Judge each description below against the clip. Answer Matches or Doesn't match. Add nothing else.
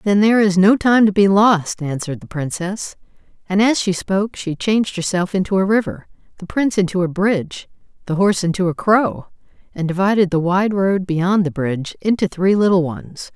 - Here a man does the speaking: Doesn't match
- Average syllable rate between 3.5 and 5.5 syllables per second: Matches